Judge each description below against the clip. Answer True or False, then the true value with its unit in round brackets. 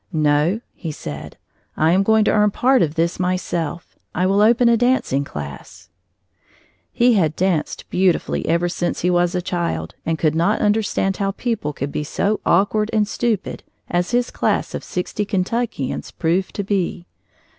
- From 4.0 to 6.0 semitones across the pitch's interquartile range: True (4.4 semitones)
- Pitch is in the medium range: True (180 Hz)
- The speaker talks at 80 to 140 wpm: False (165 wpm)